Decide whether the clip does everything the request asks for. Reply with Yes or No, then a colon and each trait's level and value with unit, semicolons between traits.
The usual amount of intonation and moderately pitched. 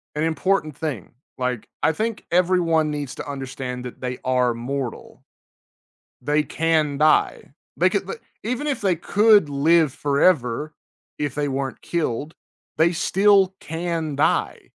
Yes: average, 4.1 semitones; medium, 150 Hz